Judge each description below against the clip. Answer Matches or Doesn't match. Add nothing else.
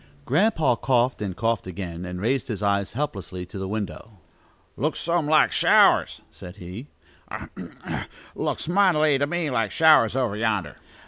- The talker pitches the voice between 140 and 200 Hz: Doesn't match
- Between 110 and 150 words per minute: Doesn't match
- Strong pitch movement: Matches